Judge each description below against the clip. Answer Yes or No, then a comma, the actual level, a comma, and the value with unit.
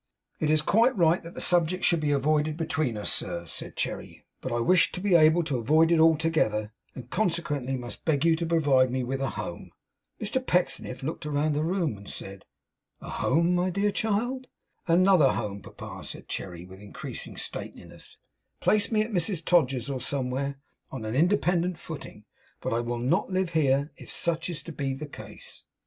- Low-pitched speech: No, medium, 155 Hz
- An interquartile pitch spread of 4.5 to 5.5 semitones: Yes, average, 5.0 semitones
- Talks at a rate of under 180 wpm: No, average, 185 wpm